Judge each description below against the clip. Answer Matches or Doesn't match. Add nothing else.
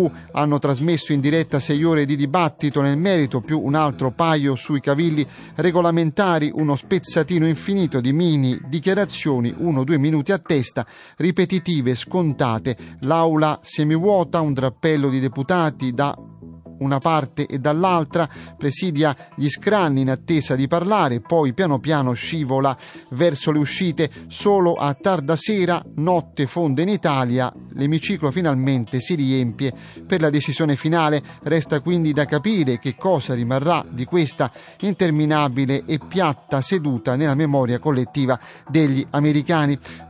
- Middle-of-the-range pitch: Matches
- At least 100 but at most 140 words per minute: Matches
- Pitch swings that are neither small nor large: Matches